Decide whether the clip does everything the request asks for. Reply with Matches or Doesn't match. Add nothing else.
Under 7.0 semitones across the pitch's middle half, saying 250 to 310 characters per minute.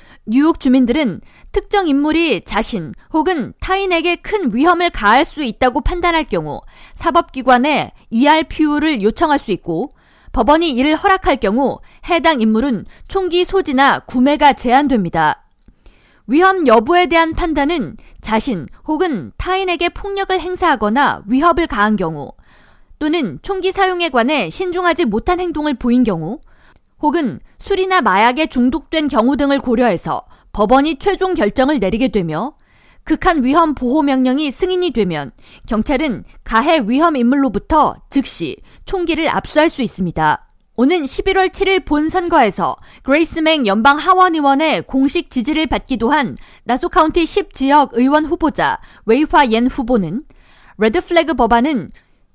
Matches